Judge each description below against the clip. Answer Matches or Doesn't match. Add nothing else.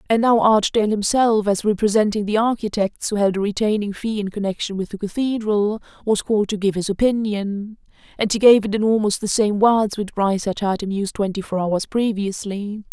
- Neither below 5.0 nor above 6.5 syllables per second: Matches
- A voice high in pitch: Matches